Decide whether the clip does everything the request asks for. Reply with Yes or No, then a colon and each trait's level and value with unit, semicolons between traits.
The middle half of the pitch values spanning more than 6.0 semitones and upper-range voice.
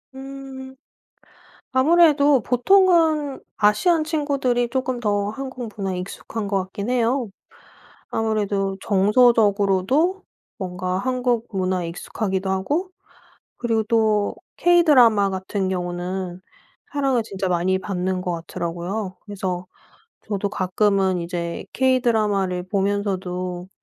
No: wide, 5.4 semitones; high, 210 Hz